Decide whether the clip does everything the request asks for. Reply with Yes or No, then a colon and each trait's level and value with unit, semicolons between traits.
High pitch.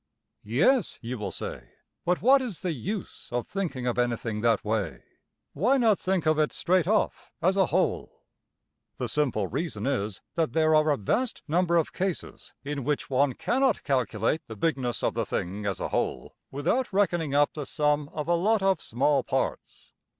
No: medium, 150 Hz